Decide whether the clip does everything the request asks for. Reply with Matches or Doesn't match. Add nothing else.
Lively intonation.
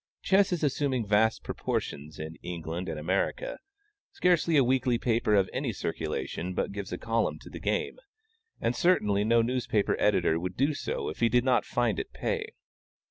Matches